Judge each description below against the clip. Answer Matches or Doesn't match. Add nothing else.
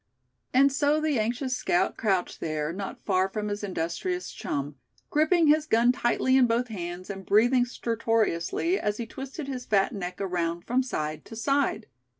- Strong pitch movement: Matches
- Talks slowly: Doesn't match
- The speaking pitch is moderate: Doesn't match